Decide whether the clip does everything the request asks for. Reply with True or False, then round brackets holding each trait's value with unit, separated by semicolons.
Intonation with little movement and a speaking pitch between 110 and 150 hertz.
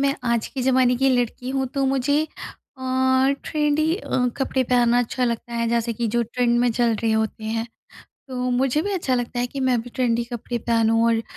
False (2.0 semitones; 245 Hz)